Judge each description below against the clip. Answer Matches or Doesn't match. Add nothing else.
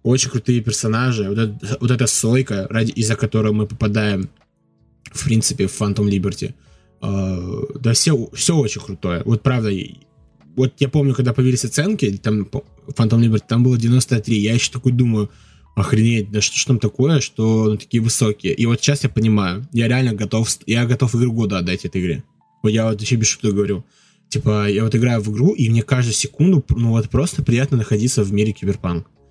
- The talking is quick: Matches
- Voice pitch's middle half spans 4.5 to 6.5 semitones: Doesn't match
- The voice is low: Matches